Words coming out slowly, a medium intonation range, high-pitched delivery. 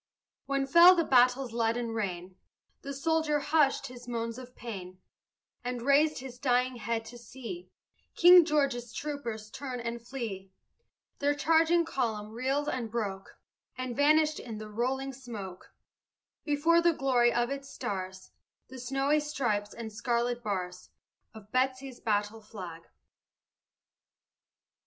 Yes: slow, 130 wpm; average, 3.9 semitones; high, 245 Hz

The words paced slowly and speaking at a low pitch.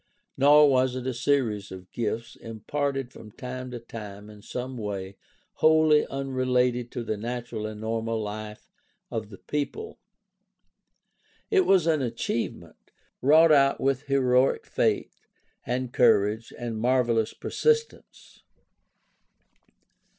Yes: slow, 125 wpm; low, 125 Hz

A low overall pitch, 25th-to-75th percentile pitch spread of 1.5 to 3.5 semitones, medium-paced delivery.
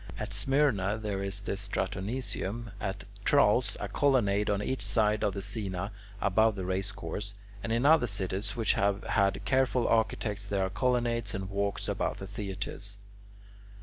Yes: low, 105 Hz; average, 2.9 semitones; average, 160 wpm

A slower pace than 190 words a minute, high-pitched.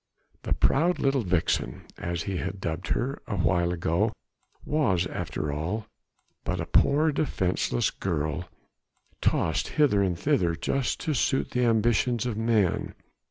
No: average, 140 wpm; low, 100 Hz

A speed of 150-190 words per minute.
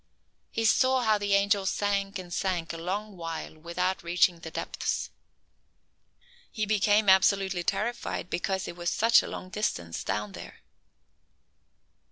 No: average, 140 wpm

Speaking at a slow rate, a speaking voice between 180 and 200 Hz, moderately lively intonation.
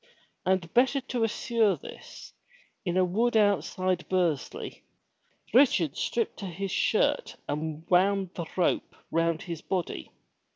Yes: slow, 125 wpm; medium, 185 Hz; average, 4.2 semitones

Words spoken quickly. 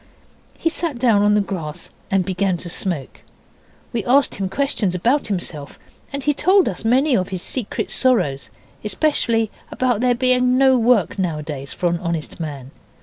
No: average, 165 wpm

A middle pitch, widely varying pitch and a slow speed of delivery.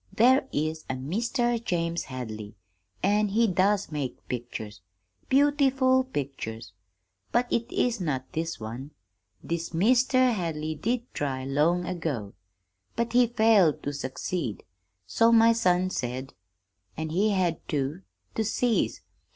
Yes: medium, 175 Hz; wide, 8.8 semitones; slow, 125 wpm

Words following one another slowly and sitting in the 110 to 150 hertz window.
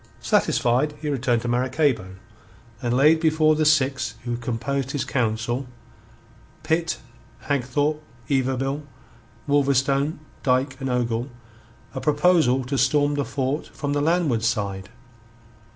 Yes: slow, 120 wpm; low, 135 Hz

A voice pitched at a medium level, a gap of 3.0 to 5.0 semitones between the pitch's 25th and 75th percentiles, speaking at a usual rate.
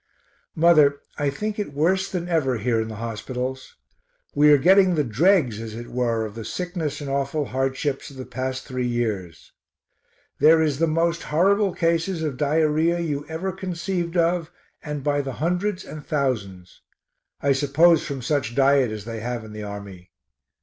No: medium, 145 Hz; wide, 5.5 semitones; average, 170 wpm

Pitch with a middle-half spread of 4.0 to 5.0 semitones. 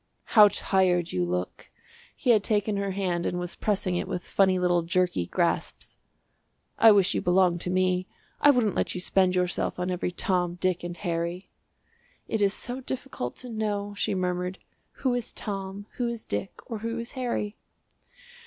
No: average, 2.9 semitones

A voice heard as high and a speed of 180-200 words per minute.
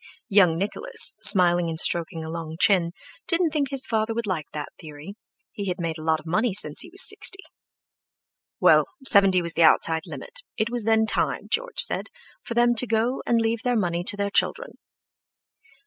Yes: high, 205 Hz; average, 190 wpm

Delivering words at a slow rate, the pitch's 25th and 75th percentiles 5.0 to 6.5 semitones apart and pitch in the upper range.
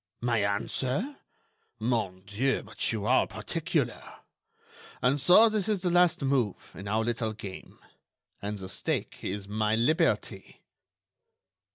No: slow, 125 wpm; wide, 5.5 semitones; low, 115 Hz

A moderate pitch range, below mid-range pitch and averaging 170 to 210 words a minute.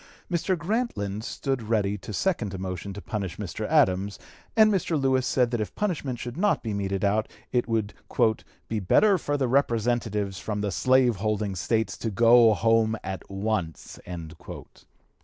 No: average, 4.4 semitones; low, 110 Hz; average, 160 wpm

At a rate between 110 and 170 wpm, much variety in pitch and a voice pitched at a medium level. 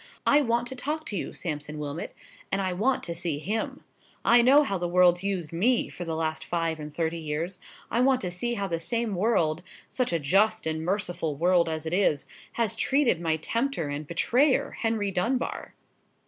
No: average, 190 wpm; wide, 6.2 semitones; medium, 180 Hz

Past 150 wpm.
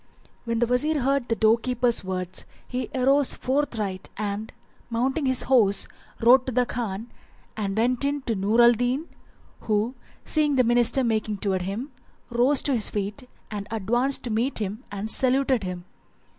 Yes: average, 170 wpm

